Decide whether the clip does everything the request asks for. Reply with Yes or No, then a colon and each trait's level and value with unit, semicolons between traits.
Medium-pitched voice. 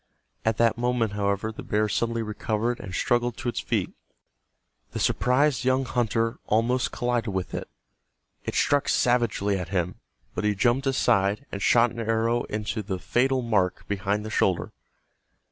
No: low, 115 Hz